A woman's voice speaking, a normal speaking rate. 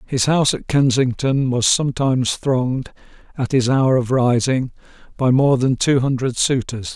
No: male; average, 155 wpm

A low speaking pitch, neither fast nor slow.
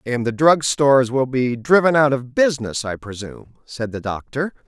Yes: low, 130 Hz; average, 195 wpm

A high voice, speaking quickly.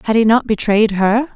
Yes: high, 220 Hz; fast, 220 wpm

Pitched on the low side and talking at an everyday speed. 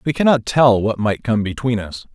No: low, 115 Hz; fast, 225 wpm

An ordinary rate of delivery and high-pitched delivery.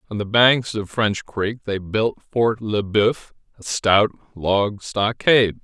No: average, 160 wpm; low, 105 Hz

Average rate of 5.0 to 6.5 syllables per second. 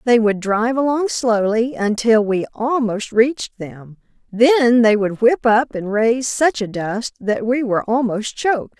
No: 4.3 syllables/s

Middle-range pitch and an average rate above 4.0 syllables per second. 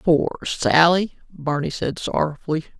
Yes: medium, 155 Hz; 4.3 syllables/s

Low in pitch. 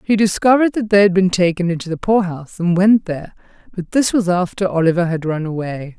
No: medium, 185 Hz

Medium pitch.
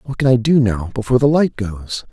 No: low, 120 Hz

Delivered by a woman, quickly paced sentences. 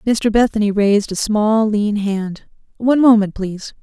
No: female; average, 155 wpm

